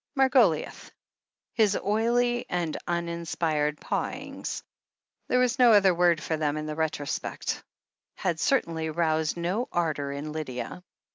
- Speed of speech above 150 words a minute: No, slow, 135 wpm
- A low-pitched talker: No, medium, 170 Hz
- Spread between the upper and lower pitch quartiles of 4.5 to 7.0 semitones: Yes, wide, 5.6 semitones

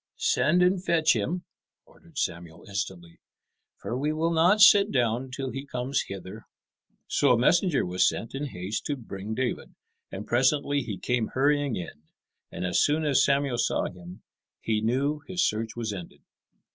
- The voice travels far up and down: Yes, wide, 5.7 semitones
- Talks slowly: No, average, 165 wpm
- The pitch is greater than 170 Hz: No, low, 125 Hz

